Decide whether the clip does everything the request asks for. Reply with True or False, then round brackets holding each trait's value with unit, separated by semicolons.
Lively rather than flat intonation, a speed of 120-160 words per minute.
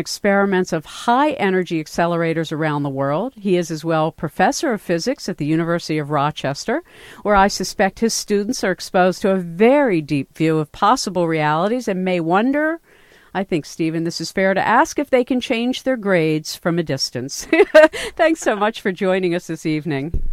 False (6.1 semitones; 185 wpm)